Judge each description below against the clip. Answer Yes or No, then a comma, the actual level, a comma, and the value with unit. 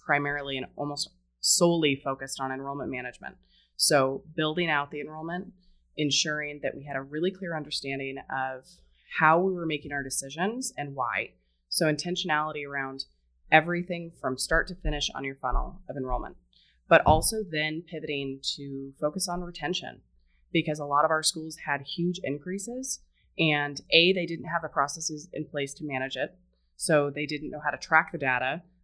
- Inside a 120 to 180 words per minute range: Yes, average, 170 wpm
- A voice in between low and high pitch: Yes, medium, 145 Hz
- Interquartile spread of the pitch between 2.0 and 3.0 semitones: No, average, 3.4 semitones